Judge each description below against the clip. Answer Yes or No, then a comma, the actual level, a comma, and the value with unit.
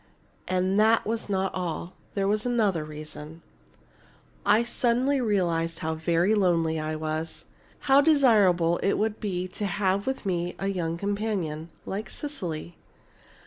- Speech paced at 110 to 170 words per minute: Yes, average, 140 wpm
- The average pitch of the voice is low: No, high, 190 Hz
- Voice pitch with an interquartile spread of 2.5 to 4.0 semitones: No, average, 4.4 semitones